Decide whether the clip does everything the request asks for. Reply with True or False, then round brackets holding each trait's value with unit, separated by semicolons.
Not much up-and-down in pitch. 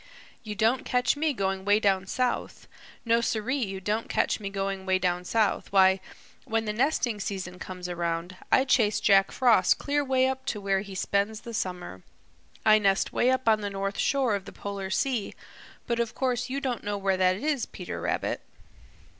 False (4.1 semitones)